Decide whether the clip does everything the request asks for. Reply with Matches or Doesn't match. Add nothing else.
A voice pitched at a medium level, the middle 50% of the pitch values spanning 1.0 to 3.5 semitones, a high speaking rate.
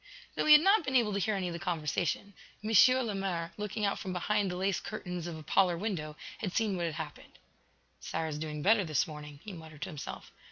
Doesn't match